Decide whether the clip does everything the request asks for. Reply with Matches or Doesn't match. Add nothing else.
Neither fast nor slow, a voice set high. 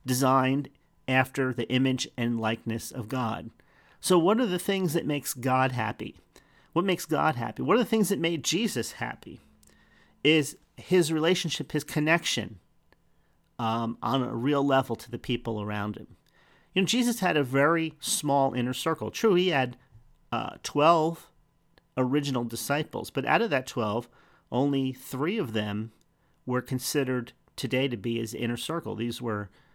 Doesn't match